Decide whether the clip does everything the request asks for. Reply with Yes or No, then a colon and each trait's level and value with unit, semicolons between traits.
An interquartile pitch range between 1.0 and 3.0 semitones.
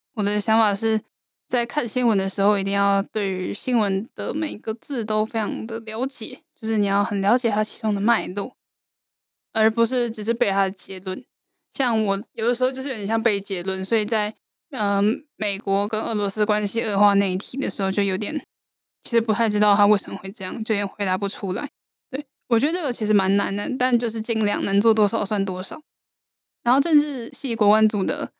Yes: average, 2.7 semitones